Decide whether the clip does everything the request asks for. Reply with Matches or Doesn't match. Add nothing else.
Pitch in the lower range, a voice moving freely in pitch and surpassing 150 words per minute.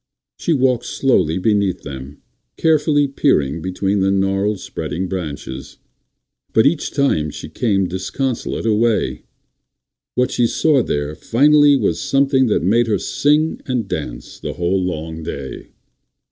Doesn't match